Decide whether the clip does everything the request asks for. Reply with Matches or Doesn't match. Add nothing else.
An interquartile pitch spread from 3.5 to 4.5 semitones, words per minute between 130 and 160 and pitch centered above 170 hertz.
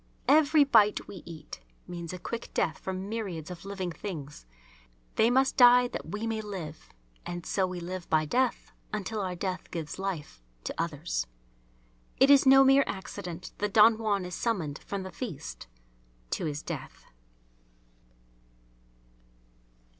Doesn't match